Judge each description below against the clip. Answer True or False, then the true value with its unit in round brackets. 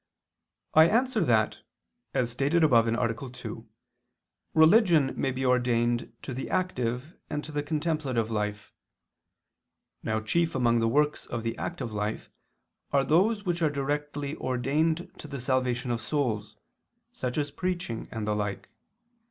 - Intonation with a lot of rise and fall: False (4.9 semitones)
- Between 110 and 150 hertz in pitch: True (135 Hz)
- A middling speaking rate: True (145 wpm)